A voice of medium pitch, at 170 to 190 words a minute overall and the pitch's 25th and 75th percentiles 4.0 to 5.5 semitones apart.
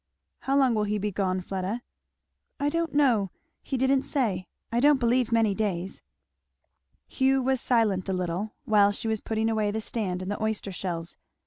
No: high, 220 Hz; average, 180 wpm; average, 4.6 semitones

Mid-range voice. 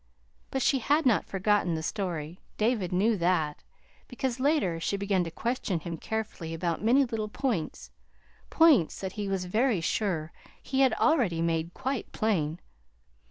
No: high, 200 Hz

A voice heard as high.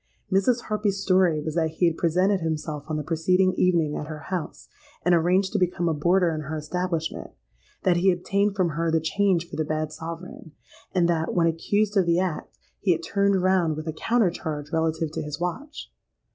No: medium, 170 Hz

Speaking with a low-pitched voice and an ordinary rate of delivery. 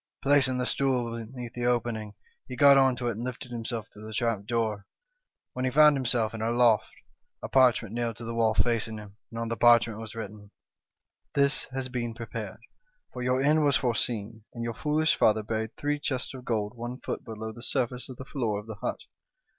No: low, 120 Hz; fast, 215 wpm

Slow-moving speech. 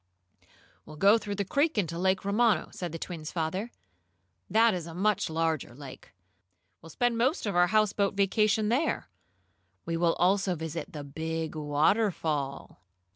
No: average, 150 wpm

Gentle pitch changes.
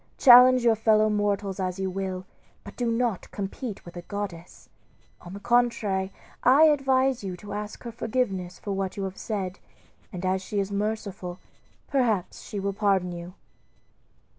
No: average, 3.5 semitones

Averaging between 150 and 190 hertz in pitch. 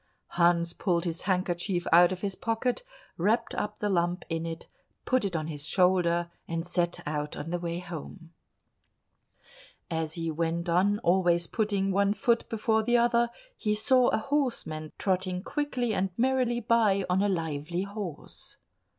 Yes: medium, 185 Hz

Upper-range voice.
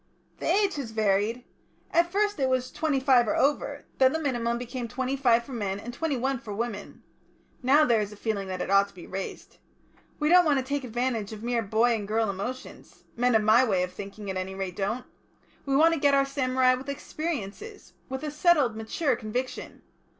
Yes: high, 245 Hz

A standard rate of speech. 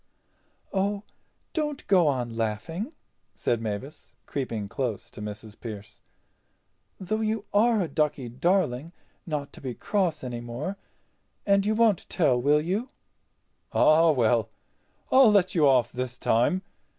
No: slow, 130 wpm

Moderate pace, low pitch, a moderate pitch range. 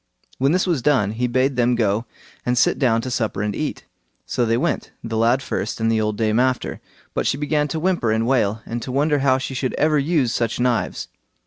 No: fast, 225 wpm; low, 125 Hz; average, 3.3 semitones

